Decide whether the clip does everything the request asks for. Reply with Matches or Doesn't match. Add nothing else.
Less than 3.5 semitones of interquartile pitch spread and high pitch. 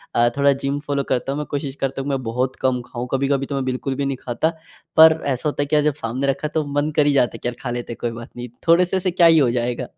Doesn't match